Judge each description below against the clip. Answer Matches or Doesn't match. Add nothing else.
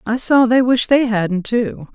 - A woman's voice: Matches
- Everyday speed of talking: Doesn't match